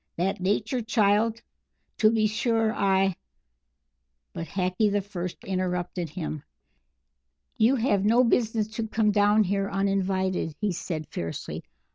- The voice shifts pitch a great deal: No, average, 3.3 semitones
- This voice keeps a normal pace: No, slow, 130 wpm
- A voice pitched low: No, high, 195 Hz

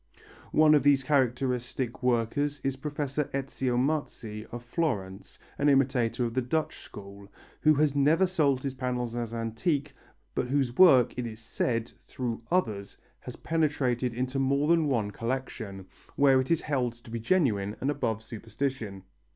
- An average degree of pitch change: Yes, average, 3.8 semitones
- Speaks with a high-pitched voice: No, low, 130 Hz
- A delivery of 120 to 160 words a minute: Yes, average, 155 wpm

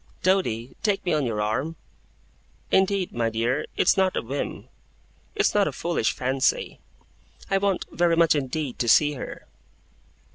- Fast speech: No, average, 150 wpm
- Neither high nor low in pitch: Yes, medium, 150 Hz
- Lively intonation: Yes, wide, 7.0 semitones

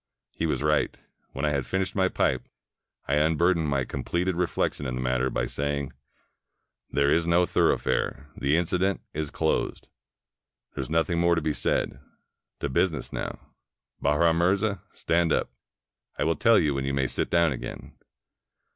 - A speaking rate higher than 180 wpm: No, average, 170 wpm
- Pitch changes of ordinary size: Yes, average, 3.4 semitones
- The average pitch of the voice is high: No, very low, 80 Hz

